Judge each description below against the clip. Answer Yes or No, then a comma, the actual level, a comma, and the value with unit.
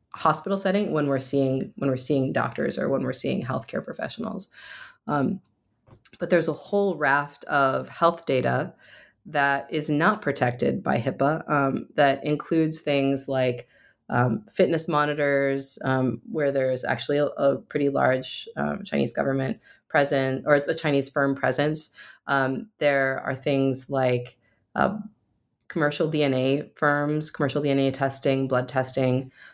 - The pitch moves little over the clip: Yes, narrow, 2.3 semitones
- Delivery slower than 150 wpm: Yes, average, 140 wpm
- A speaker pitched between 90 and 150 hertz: Yes, medium, 140 Hz